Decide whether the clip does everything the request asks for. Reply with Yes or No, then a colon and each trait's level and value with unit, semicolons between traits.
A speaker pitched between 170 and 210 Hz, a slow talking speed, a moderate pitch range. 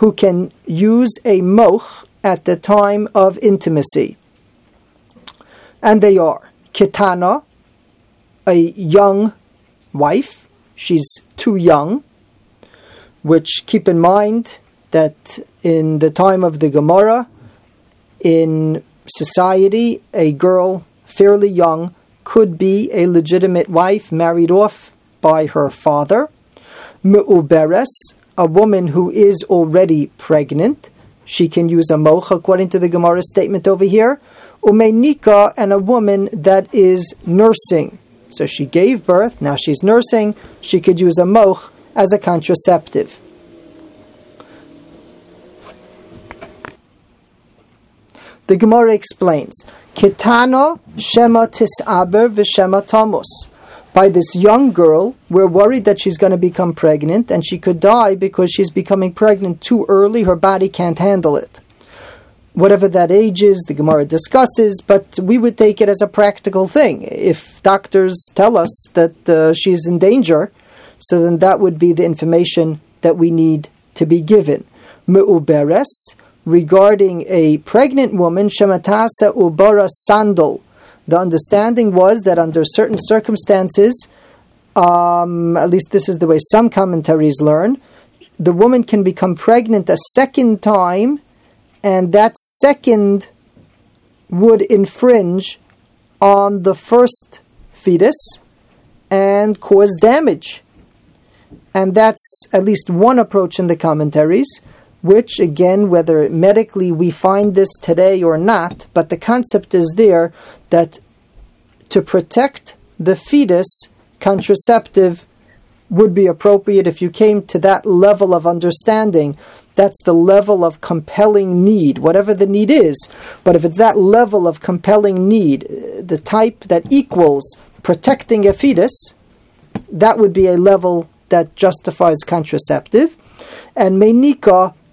Yes: high, 190 Hz; slow, 125 wpm; average, 3.6 semitones